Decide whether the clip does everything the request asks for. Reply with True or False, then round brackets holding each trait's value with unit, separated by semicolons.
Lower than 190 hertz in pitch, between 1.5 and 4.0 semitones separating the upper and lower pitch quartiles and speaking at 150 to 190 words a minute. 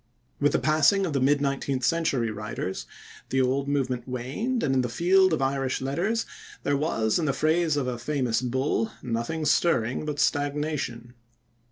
True (140 Hz; 3.6 semitones; 170 wpm)